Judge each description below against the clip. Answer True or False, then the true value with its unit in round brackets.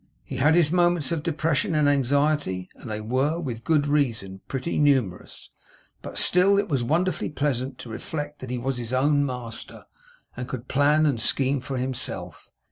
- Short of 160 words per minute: False (175 wpm)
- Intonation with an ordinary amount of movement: True (3.3 semitones)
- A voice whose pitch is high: False (140 Hz)